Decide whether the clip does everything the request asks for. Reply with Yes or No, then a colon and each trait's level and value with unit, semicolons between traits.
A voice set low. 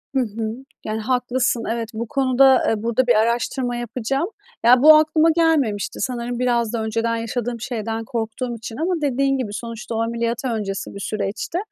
No: high, 235 Hz